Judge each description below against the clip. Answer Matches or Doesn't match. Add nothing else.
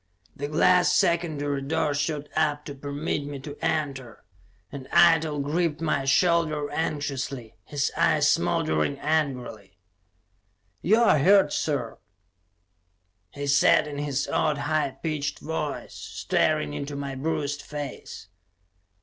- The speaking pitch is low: Doesn't match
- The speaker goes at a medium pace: Doesn't match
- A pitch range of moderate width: Doesn't match